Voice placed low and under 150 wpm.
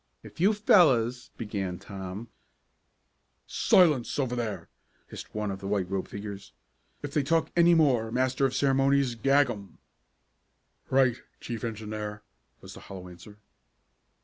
Yes: low, 120 Hz; average, 140 wpm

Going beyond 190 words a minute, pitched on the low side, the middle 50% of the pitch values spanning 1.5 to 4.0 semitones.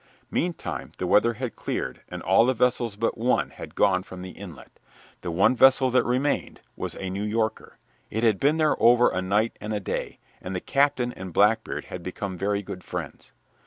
No: average, 200 wpm; low, 110 Hz; average, 4.6 semitones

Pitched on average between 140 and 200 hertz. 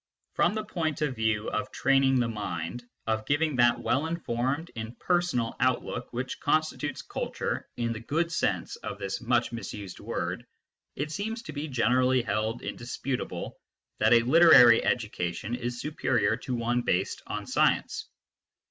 No: low, 125 Hz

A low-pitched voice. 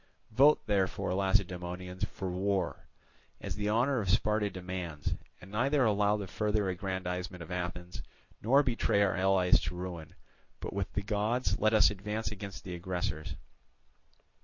Yes: very low, 95 Hz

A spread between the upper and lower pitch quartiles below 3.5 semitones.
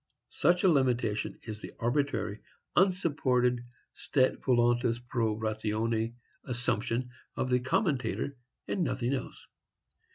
Yes: average, 3.0 semitones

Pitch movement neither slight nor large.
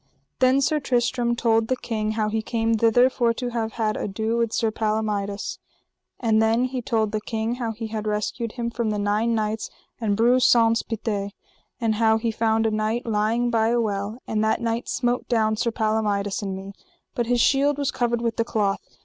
No: narrow, 1.7 semitones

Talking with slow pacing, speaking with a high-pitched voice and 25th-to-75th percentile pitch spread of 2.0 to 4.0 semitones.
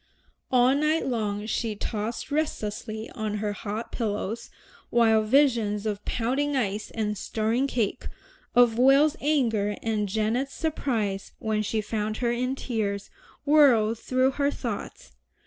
Yes: slow, 130 wpm; high, 225 Hz; average, 3.6 semitones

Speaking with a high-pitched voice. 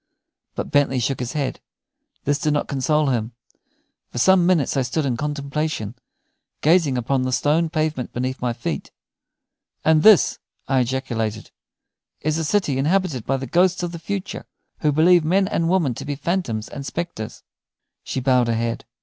No: medium, 145 Hz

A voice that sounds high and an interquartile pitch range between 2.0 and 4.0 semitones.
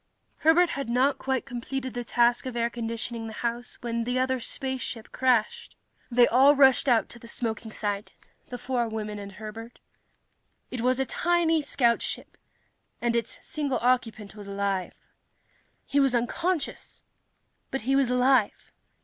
Yes: high, 245 Hz; average, 2.7 semitones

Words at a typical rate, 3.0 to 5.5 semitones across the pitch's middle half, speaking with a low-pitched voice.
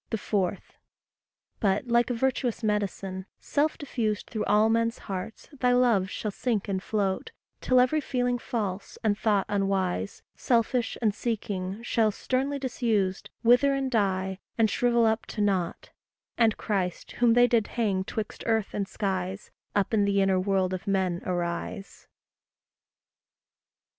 No: average, 145 wpm; average, 3.6 semitones; high, 210 Hz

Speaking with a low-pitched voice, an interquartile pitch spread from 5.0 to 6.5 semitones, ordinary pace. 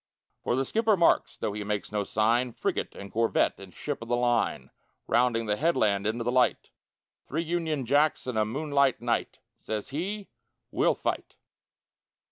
Yes: low, 120 Hz; average, 5.3 semitones; average, 165 wpm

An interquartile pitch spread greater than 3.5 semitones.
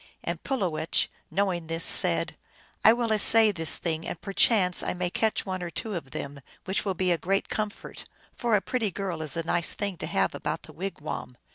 Yes: average, 3.9 semitones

